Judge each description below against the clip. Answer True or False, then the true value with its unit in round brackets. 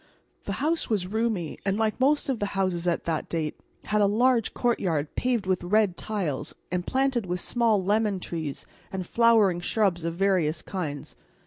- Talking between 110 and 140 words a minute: False (175 wpm)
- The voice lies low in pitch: False (195 Hz)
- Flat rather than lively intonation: False (4.2 semitones)